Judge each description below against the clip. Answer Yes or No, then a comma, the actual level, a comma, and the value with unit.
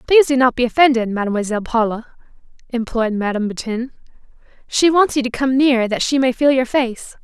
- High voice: Yes, high, 245 Hz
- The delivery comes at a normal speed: Yes, average, 185 wpm